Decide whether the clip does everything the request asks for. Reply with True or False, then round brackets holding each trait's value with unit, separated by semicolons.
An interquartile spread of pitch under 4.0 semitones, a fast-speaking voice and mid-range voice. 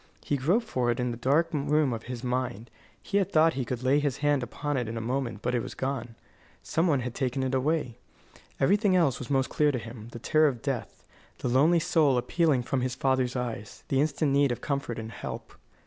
False (3.2 semitones; 225 wpm; 130 Hz)